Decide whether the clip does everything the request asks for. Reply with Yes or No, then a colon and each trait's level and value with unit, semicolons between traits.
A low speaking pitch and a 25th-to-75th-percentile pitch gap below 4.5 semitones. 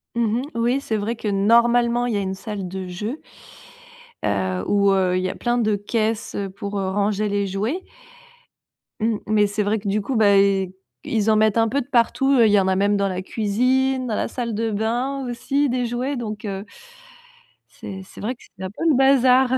No: high, 215 Hz; average, 3.4 semitones